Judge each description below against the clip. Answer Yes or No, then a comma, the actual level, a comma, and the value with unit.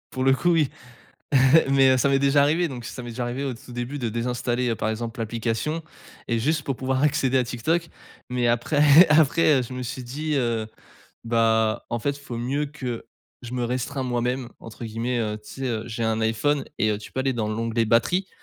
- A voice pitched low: Yes, low, 125 Hz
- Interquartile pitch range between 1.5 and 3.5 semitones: Yes, average, 3.2 semitones